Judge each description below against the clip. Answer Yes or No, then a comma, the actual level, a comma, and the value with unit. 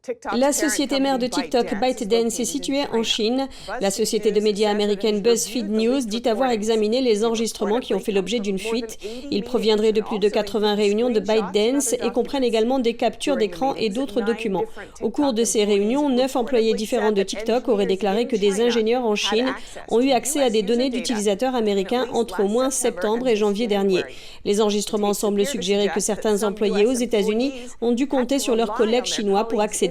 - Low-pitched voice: No, high, 230 Hz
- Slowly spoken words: No, average, 195 wpm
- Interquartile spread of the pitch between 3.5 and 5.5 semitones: No, average, 2.7 semitones